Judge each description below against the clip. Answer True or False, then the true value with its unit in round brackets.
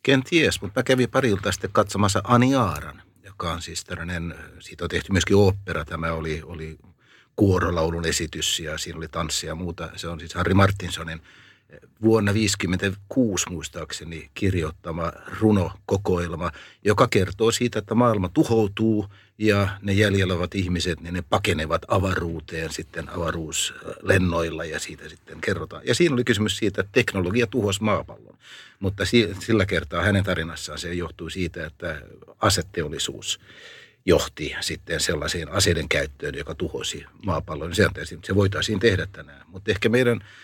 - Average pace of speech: True (140 wpm)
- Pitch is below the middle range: True (95 Hz)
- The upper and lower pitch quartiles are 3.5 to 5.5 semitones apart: True (4.0 semitones)